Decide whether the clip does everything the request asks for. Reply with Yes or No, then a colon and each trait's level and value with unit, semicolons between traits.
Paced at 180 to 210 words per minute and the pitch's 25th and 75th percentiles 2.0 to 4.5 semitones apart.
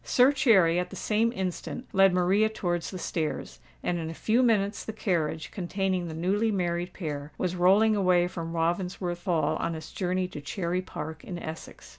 Yes: average, 185 wpm; average, 2.8 semitones